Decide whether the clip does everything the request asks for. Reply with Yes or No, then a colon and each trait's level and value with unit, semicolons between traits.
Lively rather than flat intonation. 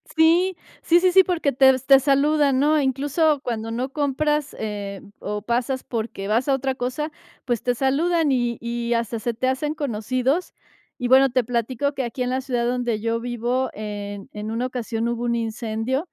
No: average, 3.3 semitones